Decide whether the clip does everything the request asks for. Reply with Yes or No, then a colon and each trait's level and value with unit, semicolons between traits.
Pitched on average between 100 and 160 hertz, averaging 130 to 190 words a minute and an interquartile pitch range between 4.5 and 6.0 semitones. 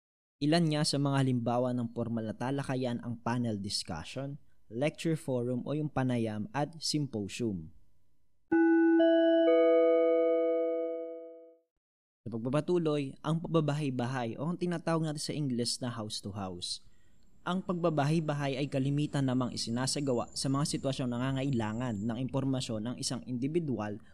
No: low, 135 Hz; average, 115 wpm; average, 5.2 semitones